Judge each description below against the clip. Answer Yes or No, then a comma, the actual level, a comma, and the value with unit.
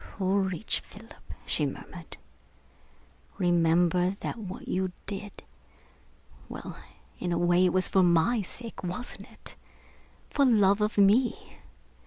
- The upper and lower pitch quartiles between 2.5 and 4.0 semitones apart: Yes, average, 2.9 semitones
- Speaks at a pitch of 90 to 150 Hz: No, high, 190 Hz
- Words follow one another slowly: Yes, slow, 120 wpm